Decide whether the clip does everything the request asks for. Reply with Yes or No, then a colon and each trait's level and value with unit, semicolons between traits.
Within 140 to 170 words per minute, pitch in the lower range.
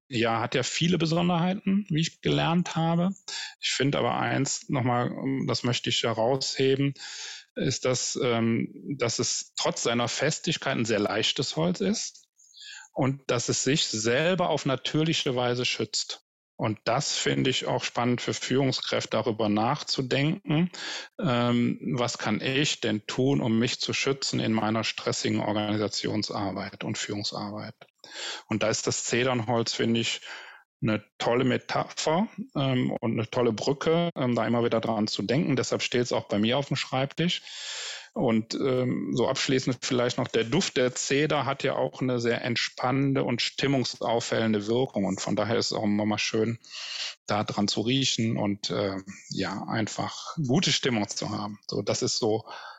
Yes: average, 160 wpm; low, 125 Hz